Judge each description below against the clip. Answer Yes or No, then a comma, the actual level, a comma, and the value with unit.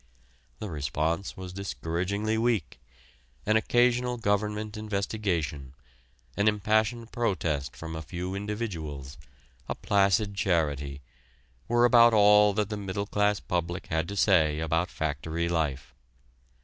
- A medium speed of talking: No, slow, 120 wpm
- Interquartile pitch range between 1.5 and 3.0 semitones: No, average, 4.8 semitones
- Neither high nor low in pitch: No, low, 100 Hz